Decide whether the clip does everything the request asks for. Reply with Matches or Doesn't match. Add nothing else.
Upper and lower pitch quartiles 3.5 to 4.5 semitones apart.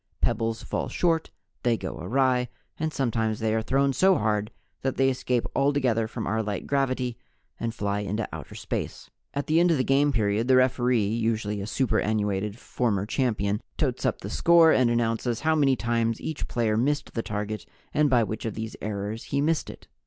Matches